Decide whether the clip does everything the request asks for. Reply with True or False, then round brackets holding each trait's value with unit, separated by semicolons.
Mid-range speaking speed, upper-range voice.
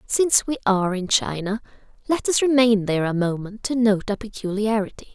True (175 wpm; 215 Hz)